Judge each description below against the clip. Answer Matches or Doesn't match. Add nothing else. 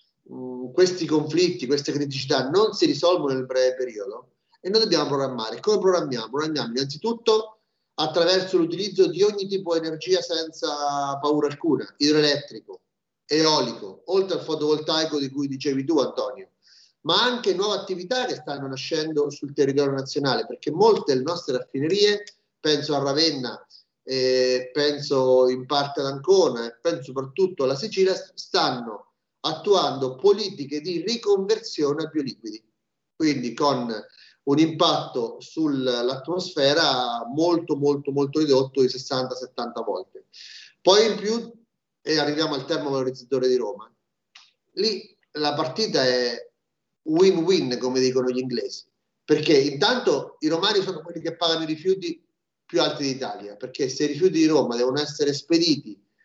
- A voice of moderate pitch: Matches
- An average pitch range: Doesn't match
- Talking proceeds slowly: Doesn't match